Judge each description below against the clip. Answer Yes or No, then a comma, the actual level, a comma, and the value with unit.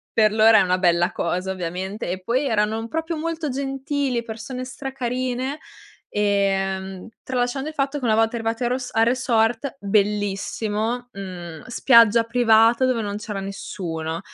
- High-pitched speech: Yes, high, 225 Hz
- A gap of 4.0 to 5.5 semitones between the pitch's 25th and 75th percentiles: Yes, average, 4.3 semitones